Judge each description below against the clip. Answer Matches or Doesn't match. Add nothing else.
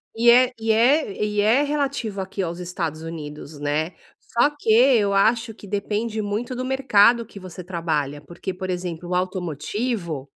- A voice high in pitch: Matches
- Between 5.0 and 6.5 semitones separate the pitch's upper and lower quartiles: Matches